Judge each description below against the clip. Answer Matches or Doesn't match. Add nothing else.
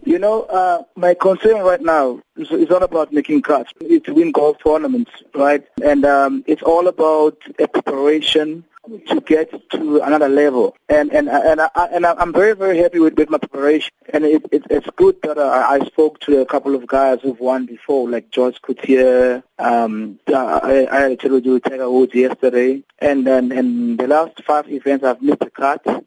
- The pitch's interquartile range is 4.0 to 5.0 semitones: Matches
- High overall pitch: Doesn't match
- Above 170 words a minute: Matches